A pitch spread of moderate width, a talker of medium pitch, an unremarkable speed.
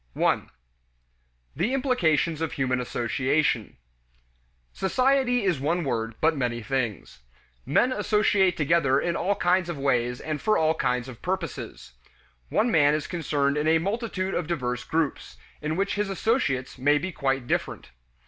No: wide, 6.1 semitones; medium, 155 Hz; average, 150 wpm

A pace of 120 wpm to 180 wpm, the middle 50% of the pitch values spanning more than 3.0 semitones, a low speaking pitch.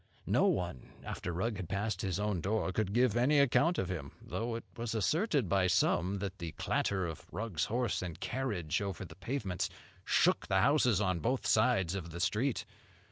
No: average, 190 wpm; average, 4.7 semitones; low, 100 Hz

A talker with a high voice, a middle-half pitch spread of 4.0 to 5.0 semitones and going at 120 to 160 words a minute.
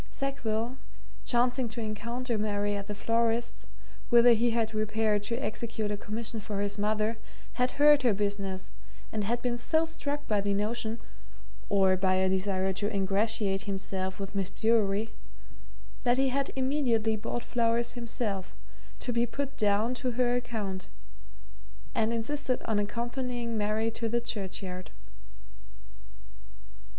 No: high, 220 Hz; average, 2.9 semitones; average, 140 wpm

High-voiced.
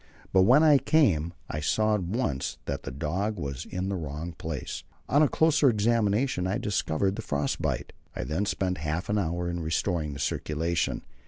No: very low, 90 Hz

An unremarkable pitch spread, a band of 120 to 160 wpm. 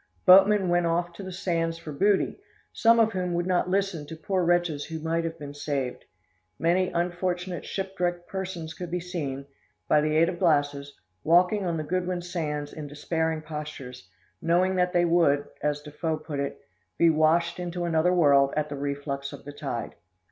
No: average, 3.2 semitones; average, 180 wpm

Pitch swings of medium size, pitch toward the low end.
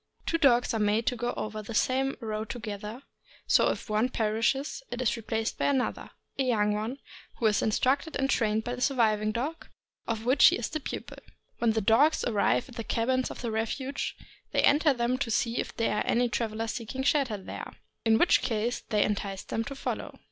No: average, 3.2 semitones; high, 230 Hz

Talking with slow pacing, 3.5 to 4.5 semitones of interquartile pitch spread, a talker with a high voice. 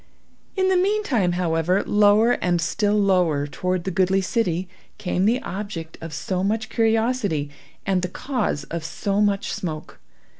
No: average, 150 wpm; average, 4.1 semitones; high, 195 Hz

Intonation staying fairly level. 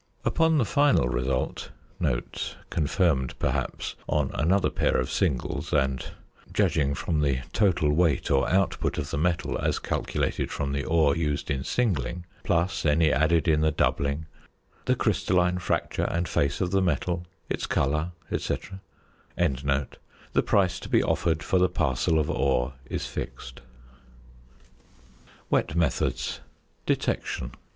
No: average, 4.3 semitones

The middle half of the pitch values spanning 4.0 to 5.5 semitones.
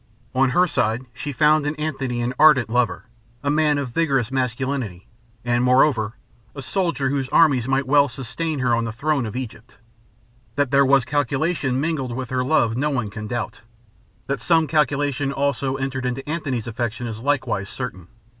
No: average, 3.0 semitones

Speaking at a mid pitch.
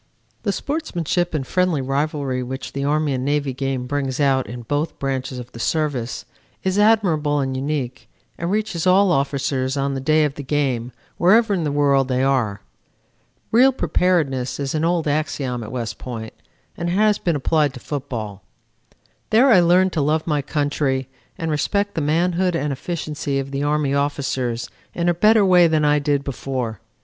Yes: medium, 145 Hz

